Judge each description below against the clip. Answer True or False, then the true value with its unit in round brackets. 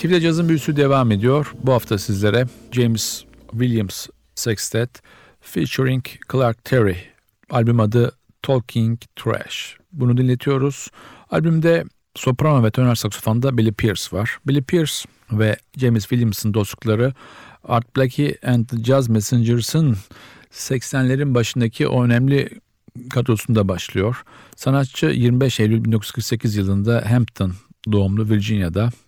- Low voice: True (120 Hz)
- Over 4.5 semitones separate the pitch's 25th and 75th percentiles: False (3.1 semitones)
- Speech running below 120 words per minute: True (110 wpm)